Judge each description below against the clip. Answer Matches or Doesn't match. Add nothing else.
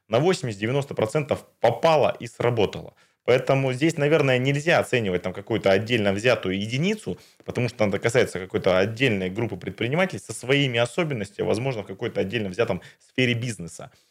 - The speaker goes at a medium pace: Matches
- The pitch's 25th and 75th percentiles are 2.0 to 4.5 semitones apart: Doesn't match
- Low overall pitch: Matches